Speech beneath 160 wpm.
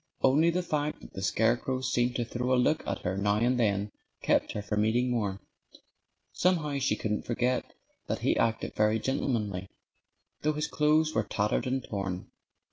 No: average, 175 wpm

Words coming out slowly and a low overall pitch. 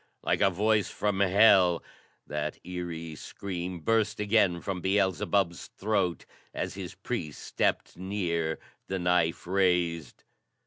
Yes: slow, 120 wpm; very low, 90 Hz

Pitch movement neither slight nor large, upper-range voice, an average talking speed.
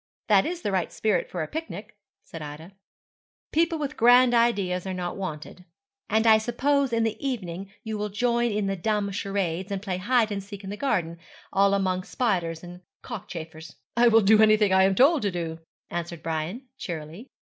Yes: average, 4.4 semitones; high, 200 Hz; average, 190 wpm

